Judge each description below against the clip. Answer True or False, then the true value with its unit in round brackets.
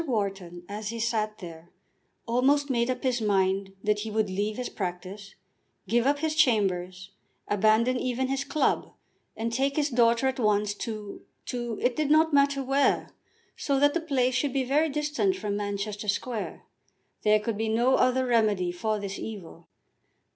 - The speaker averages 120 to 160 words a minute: False (170 wpm)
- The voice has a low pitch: False (230 Hz)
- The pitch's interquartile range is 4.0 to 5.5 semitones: True (4.4 semitones)